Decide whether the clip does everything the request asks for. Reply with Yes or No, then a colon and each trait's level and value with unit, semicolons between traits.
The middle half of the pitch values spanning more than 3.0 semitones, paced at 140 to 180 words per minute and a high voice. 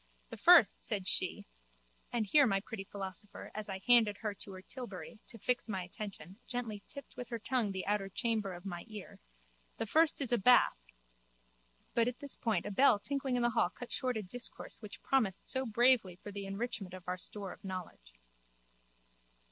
No: average, 4.1 semitones; average, 190 wpm; high, 210 Hz